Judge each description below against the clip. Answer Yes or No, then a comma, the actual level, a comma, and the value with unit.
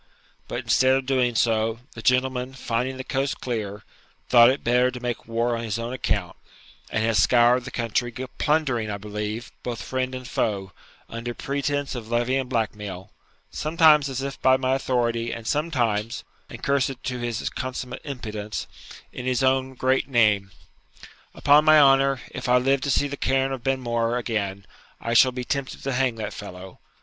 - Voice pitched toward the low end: Yes, low, 125 Hz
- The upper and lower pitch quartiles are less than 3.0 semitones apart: Yes, narrow, 2.5 semitones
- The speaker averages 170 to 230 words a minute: Yes, average, 175 wpm